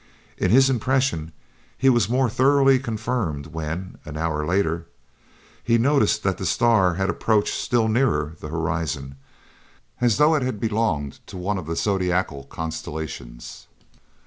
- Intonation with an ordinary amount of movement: No, wide, 7.0 semitones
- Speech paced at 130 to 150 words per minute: Yes, average, 145 wpm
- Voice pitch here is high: No, very low, 95 Hz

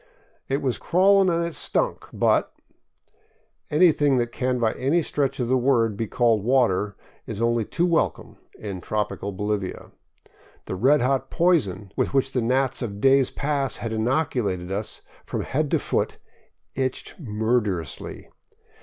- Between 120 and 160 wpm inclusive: Yes, average, 155 wpm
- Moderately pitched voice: No, low, 125 Hz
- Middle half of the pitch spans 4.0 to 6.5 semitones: Yes, average, 4.7 semitones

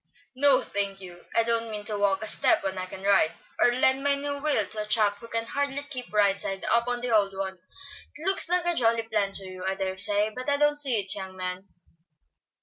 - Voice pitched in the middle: No, high, 215 Hz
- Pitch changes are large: No, average, 5.0 semitones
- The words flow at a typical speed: No, fast, 240 wpm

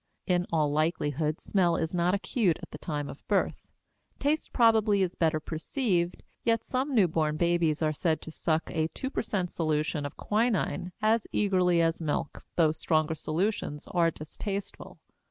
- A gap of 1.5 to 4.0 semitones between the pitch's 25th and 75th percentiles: No, average, 4.4 semitones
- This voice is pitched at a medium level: Yes, medium, 170 Hz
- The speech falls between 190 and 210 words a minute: No, average, 160 wpm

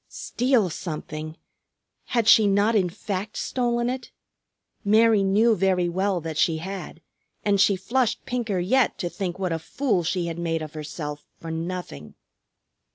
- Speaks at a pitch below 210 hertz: Yes, high, 190 Hz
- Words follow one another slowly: No, average, 155 wpm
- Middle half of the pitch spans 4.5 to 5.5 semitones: Yes, average, 4.9 semitones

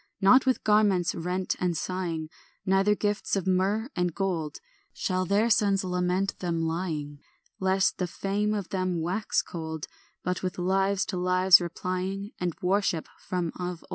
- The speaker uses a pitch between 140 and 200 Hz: Yes, medium, 185 Hz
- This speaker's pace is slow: No, average, 160 wpm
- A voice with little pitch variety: Yes, narrow, 1.9 semitones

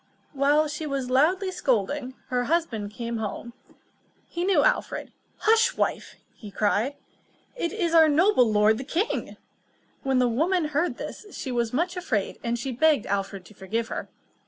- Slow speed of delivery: No, average, 165 wpm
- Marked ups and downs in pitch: Yes, wide, 6.4 semitones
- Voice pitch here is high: Yes, very high, 270 Hz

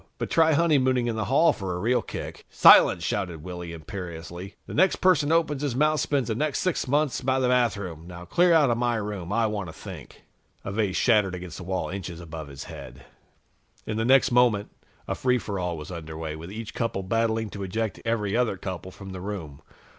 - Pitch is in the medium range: No, low, 105 Hz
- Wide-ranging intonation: Yes, wide, 6.0 semitones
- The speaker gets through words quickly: Yes, fast, 215 wpm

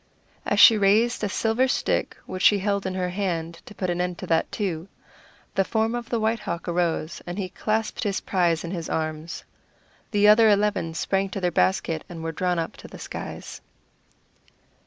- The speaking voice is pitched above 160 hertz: Yes, high, 190 Hz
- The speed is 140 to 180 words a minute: No, average, 195 wpm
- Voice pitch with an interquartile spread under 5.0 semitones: Yes, average, 3.7 semitones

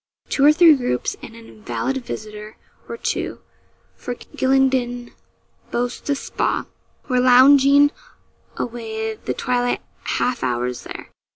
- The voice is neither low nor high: No, high, 245 Hz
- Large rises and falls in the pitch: No, average, 3.0 semitones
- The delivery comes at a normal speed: No, slow, 120 wpm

